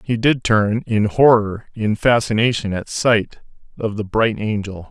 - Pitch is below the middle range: Yes, low, 110 Hz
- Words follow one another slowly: No, average, 160 wpm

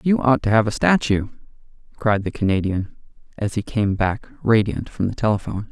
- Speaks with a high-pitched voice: No, low, 110 Hz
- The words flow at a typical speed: Yes, average, 180 wpm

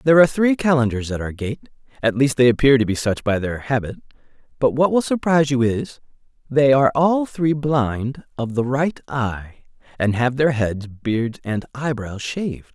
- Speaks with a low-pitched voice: Yes, low, 130 Hz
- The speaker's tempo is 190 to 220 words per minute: Yes, average, 195 wpm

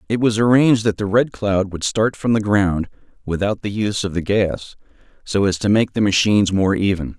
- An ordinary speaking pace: No, fast, 215 wpm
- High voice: No, low, 105 Hz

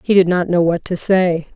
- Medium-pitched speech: Yes, medium, 175 Hz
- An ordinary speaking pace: No, fast, 270 wpm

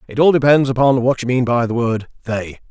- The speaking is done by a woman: No, male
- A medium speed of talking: No, fast, 245 wpm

